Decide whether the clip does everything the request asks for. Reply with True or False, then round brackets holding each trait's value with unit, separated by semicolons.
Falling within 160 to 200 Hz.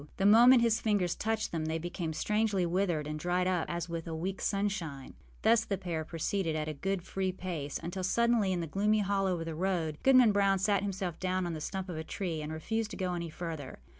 True (185 Hz)